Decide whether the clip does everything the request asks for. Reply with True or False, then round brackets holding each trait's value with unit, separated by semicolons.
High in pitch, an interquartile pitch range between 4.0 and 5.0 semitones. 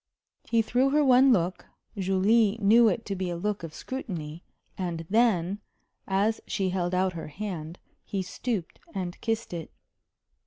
True (195 Hz; 4.3 semitones)